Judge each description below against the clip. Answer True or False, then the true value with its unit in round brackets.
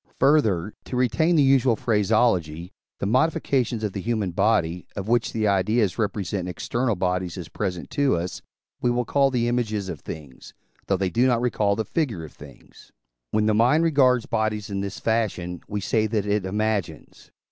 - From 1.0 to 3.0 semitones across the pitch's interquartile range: False (4.4 semitones)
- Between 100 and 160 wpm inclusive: False (180 wpm)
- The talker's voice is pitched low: True (110 Hz)